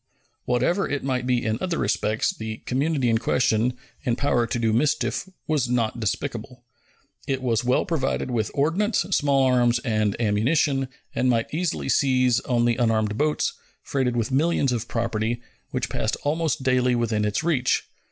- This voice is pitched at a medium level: No, low, 125 Hz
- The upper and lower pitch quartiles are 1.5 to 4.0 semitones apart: Yes, average, 3.2 semitones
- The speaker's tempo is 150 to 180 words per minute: Yes, average, 160 wpm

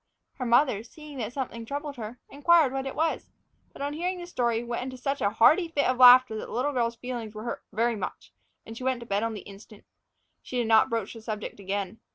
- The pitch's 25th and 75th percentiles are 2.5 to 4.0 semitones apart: Yes, average, 3.7 semitones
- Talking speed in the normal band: No, fast, 240 wpm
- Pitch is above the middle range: Yes, high, 240 Hz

